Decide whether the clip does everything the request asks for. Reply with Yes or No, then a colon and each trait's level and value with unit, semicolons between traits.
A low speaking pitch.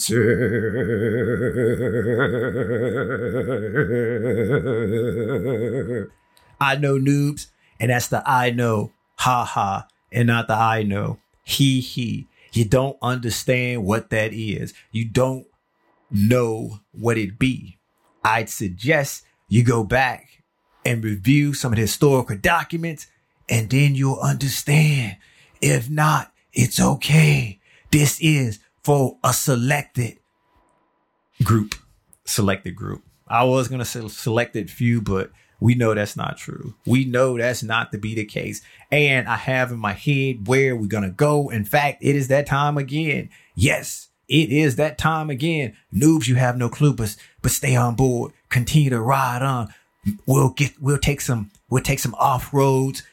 Yes: low, 125 Hz